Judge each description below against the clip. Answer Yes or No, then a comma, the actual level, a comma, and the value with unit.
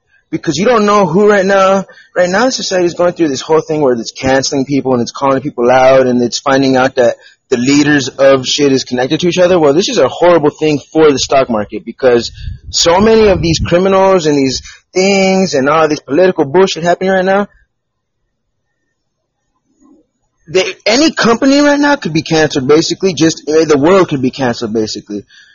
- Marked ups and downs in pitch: Yes, wide, 6.1 semitones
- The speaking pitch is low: No, medium, 160 Hz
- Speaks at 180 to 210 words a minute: Yes, average, 195 wpm